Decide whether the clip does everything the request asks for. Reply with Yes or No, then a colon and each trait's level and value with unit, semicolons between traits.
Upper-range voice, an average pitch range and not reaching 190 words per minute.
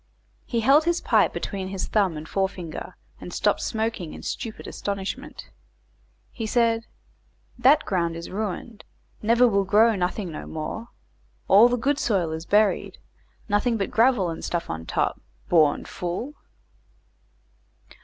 Yes: high, 205 Hz; average, 4.6 semitones; average, 140 wpm